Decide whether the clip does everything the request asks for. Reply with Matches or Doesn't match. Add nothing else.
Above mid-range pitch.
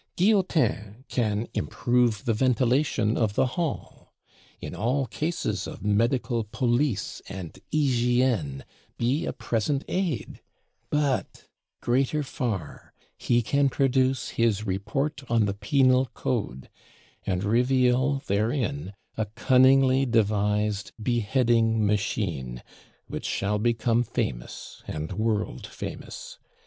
Doesn't match